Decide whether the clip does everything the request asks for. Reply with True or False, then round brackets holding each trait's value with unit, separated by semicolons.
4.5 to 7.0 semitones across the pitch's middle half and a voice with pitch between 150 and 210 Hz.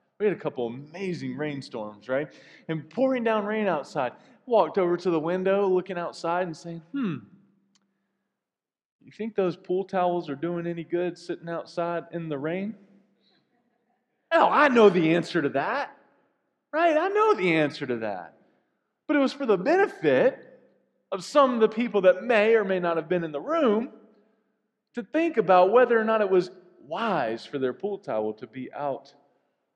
True (5.1 semitones; 190 Hz)